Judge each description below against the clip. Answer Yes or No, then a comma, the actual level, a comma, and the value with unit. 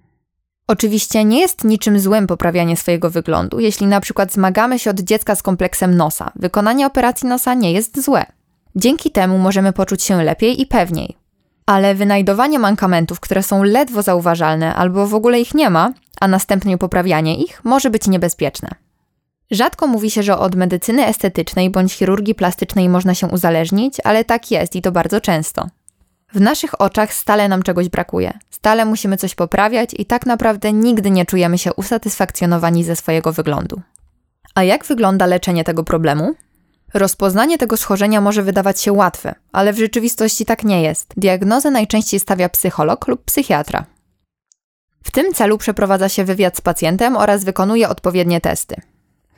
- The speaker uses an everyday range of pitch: Yes, average, 3.4 semitones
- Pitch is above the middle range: Yes, high, 200 Hz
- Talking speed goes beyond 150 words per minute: Yes, fast, 160 wpm